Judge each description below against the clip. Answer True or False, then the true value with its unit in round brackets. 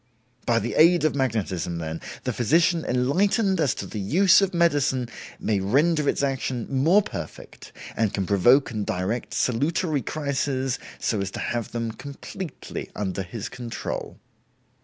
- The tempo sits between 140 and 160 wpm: True (150 wpm)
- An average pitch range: False (6.2 semitones)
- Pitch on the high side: False (130 Hz)